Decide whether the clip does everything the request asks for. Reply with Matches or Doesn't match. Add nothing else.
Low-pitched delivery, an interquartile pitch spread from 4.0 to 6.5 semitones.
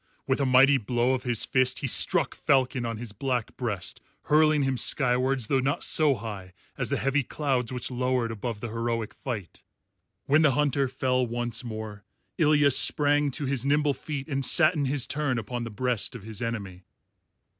Doesn't match